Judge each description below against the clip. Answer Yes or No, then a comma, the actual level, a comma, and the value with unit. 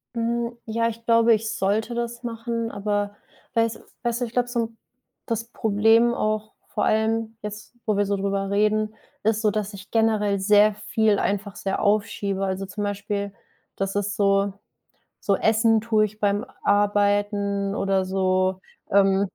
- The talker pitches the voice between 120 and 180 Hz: No, high, 210 Hz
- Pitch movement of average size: No, narrow, 2.0 semitones